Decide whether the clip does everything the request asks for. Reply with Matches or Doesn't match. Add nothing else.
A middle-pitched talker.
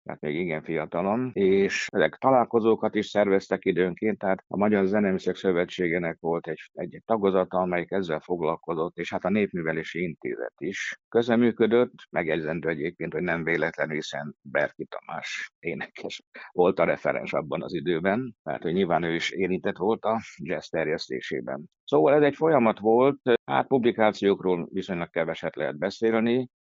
Doesn't match